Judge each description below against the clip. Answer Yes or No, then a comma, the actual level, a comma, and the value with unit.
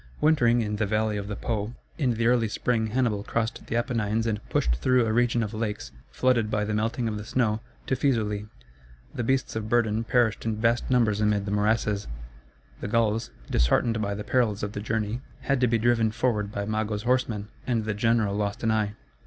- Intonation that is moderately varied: No, narrow, 2.1 semitones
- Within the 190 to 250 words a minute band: Yes, average, 200 wpm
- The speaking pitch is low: Yes, low, 110 Hz